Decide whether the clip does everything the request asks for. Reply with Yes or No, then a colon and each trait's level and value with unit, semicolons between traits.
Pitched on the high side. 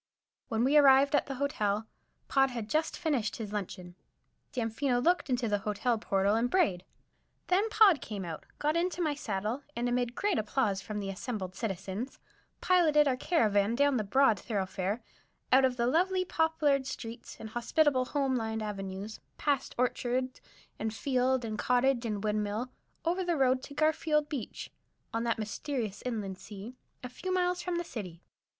Yes: high, 245 Hz